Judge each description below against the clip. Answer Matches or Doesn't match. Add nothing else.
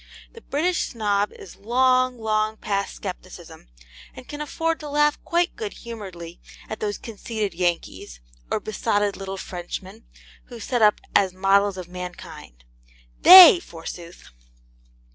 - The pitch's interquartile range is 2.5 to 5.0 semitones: Doesn't match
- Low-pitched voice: Doesn't match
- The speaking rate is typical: Doesn't match